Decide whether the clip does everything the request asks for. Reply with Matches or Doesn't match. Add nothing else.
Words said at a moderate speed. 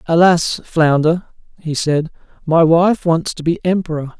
Matches